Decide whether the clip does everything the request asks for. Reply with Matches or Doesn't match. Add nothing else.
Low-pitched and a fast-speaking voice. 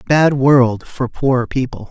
Doesn't match